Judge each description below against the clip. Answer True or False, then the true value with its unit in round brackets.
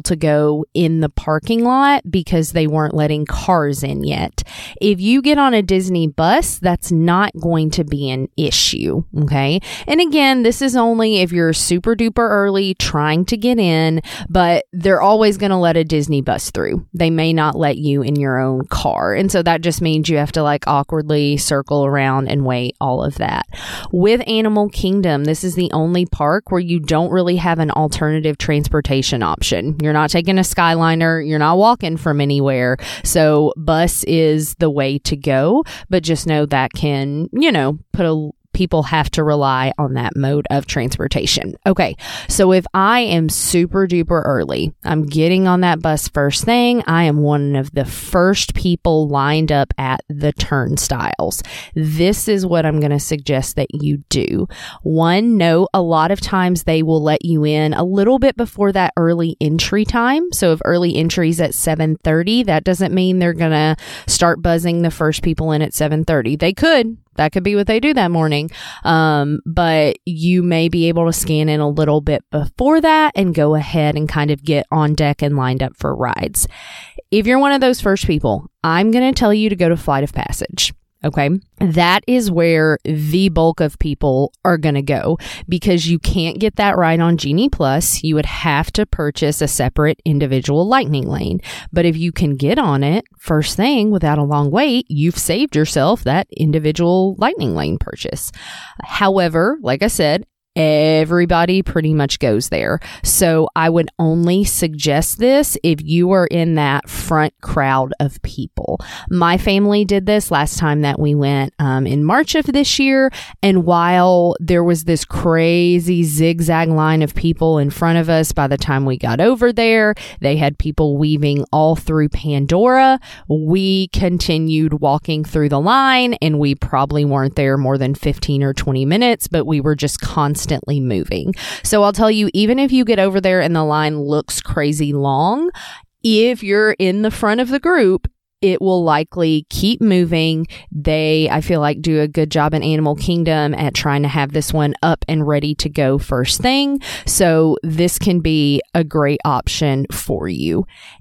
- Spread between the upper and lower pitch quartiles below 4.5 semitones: True (3.8 semitones)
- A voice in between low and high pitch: True (160 Hz)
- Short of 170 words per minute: False (185 wpm)